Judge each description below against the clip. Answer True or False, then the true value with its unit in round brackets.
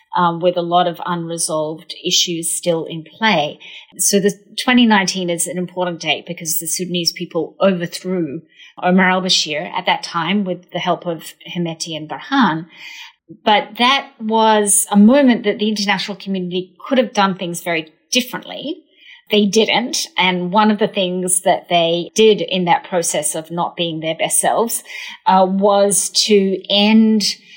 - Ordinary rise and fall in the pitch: True (3.5 semitones)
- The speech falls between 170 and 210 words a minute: False (160 wpm)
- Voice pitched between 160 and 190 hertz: True (185 Hz)